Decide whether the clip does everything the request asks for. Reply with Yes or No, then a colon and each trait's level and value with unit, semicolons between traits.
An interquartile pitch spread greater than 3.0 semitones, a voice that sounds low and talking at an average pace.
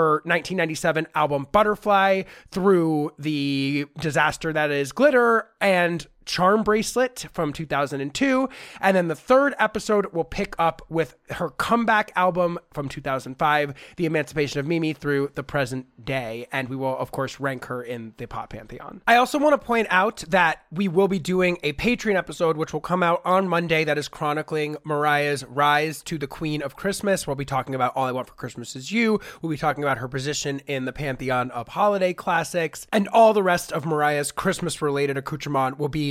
No: average, 4.8 semitones; medium, 155 Hz; average, 185 wpm